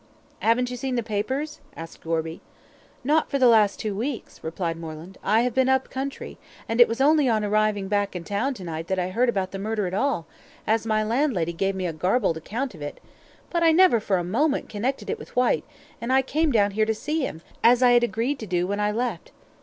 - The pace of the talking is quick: Yes, fast, 230 wpm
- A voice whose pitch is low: No, high, 220 Hz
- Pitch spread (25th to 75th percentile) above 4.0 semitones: Yes, average, 5.2 semitones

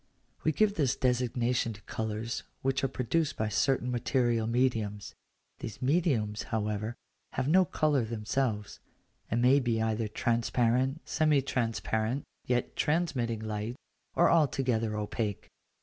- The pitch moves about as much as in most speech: Yes, average, 3.4 semitones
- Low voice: Yes, low, 120 Hz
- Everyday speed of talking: No, slow, 125 wpm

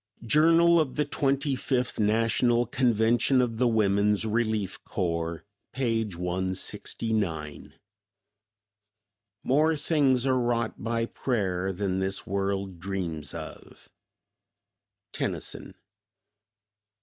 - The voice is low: Yes, low, 110 Hz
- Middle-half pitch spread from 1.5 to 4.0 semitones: No, average, 4.9 semitones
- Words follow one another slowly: Yes, slow, 90 wpm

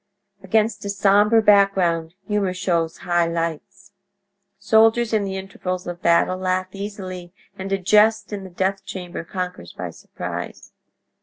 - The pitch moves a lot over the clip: No, narrow, 2.4 semitones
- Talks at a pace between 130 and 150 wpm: Yes, average, 140 wpm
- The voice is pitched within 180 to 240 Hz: Yes, high, 190 Hz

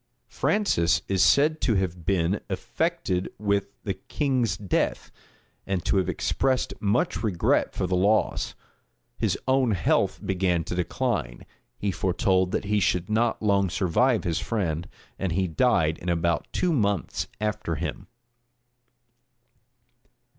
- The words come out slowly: Yes, slow, 130 wpm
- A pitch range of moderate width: Yes, average, 3.7 semitones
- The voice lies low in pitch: Yes, very low, 95 Hz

